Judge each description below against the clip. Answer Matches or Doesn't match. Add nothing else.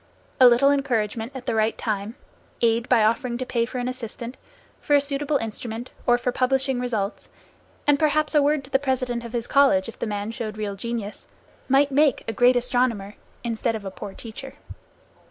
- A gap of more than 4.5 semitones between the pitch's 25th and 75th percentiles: Doesn't match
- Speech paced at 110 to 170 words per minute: Doesn't match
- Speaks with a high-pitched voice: Matches